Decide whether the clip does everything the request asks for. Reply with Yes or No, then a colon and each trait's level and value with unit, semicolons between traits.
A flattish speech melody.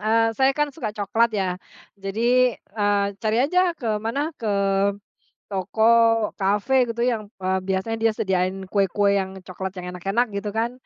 No: average, 3.1 semitones